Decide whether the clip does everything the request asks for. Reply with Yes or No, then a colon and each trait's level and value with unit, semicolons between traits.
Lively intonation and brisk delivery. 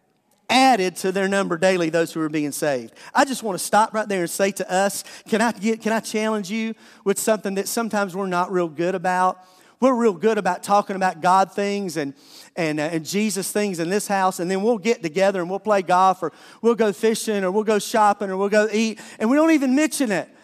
No: average, 3.1 semitones; fast, 240 wpm